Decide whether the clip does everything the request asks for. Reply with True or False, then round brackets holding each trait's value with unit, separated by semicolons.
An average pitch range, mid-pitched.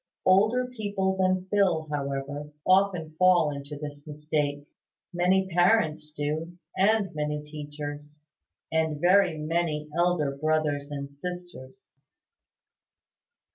True (3.9 semitones; 155 Hz)